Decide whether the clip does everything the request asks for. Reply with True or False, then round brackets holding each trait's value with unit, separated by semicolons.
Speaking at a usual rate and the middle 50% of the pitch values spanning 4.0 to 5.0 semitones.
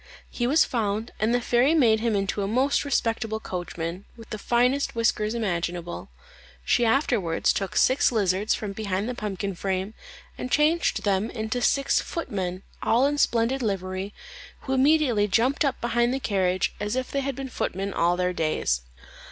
True (170 wpm; 4.6 semitones)